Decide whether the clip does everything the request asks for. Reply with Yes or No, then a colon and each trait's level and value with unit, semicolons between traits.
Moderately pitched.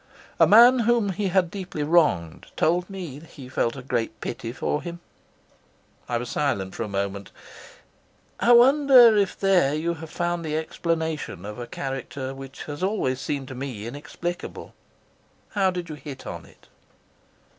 Yes: medium, 155 Hz